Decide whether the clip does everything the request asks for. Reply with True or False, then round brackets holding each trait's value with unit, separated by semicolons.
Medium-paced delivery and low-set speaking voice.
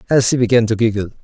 True (195 wpm; 115 Hz)